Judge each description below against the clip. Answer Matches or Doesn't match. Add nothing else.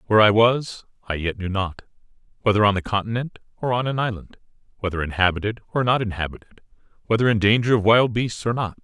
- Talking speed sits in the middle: Matches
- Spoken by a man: Matches